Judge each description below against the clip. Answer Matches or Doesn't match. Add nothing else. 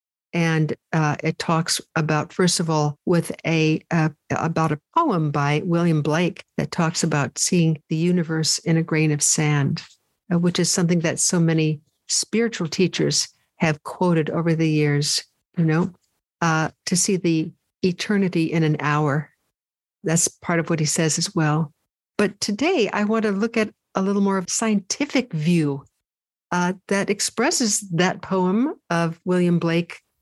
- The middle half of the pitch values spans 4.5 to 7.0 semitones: Doesn't match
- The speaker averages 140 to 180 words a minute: Matches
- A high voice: Doesn't match